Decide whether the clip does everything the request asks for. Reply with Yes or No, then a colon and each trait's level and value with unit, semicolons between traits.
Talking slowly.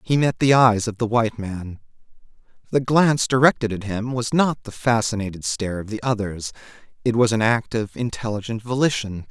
No: average, 180 wpm